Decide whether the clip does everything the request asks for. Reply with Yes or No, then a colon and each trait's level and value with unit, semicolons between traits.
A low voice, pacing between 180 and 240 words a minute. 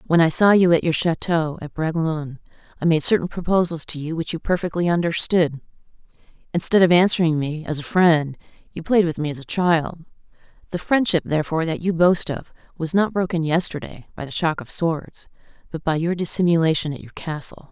No: medium, 165 Hz; average, 190 wpm